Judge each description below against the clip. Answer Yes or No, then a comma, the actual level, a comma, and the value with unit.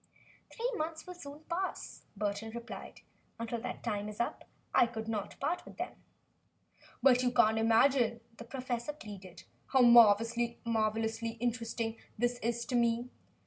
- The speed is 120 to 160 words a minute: Yes, average, 145 wpm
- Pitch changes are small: Yes, narrow, 2.0 semitones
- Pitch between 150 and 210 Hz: No, high, 235 Hz